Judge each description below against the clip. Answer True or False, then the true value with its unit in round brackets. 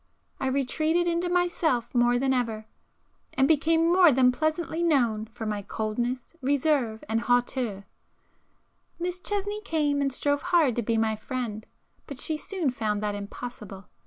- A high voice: True (260 Hz)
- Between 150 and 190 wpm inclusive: False (140 wpm)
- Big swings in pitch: True (6.2 semitones)